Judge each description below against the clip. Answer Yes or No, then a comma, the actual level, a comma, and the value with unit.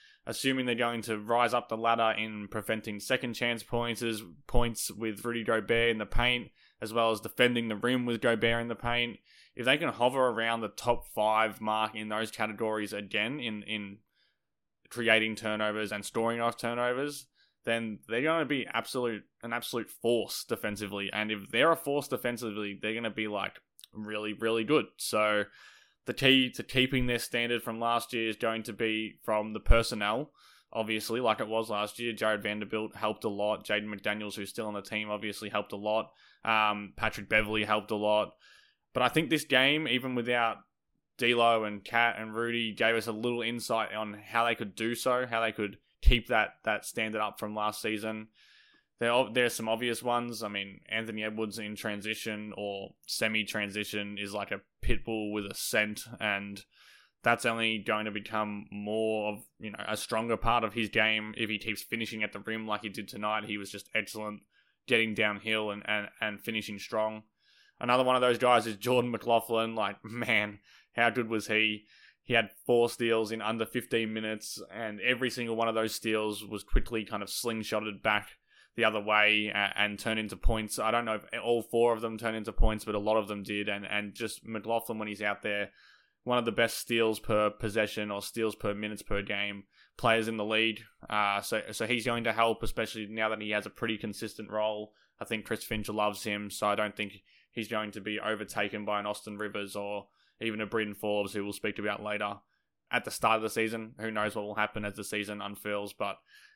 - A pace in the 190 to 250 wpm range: Yes, average, 200 wpm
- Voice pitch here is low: Yes, low, 110 Hz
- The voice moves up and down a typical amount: No, narrow, 1.7 semitones